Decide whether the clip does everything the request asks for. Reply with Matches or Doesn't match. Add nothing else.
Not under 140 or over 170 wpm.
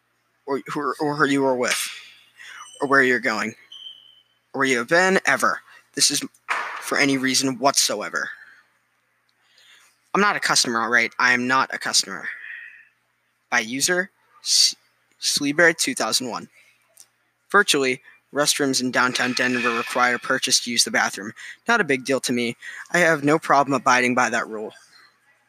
Matches